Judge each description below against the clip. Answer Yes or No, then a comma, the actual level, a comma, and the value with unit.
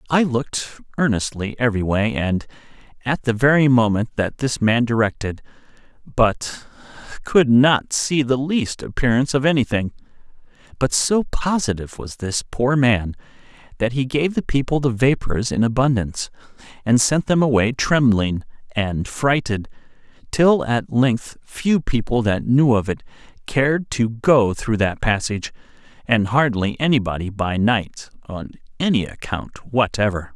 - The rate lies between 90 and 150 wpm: Yes, average, 140 wpm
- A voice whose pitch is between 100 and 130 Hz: Yes, low, 120 Hz